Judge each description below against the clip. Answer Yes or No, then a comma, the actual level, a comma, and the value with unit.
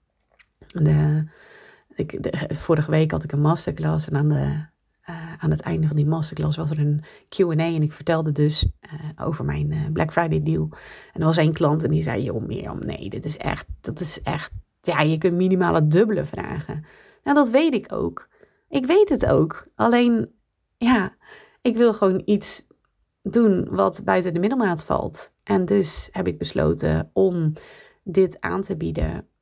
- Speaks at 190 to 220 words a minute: No, average, 180 wpm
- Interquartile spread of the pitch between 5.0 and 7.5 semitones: No, average, 4.3 semitones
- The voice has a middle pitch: Yes, medium, 160 Hz